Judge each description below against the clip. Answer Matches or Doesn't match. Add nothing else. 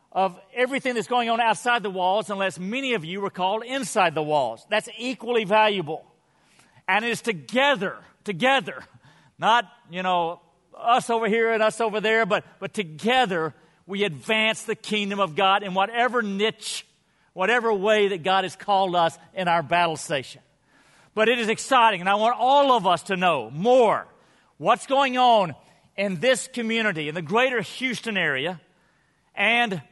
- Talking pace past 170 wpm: Doesn't match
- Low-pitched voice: Doesn't match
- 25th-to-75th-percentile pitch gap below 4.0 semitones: Doesn't match